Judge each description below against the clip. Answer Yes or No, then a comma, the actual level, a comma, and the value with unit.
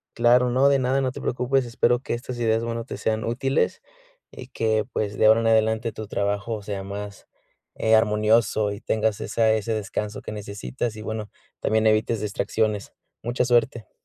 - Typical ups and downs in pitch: No, narrow, 2.0 semitones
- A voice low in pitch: Yes, low, 110 Hz